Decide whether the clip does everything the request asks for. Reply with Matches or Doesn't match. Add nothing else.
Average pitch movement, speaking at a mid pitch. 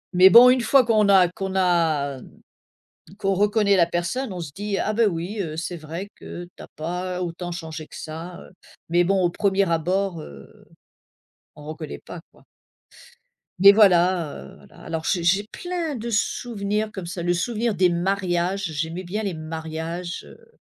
Matches